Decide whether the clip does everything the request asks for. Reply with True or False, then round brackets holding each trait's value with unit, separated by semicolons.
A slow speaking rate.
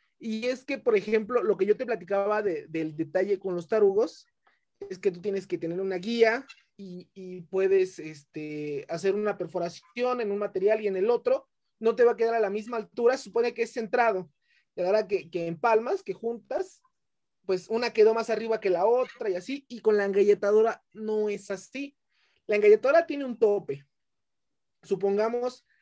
False (190 wpm)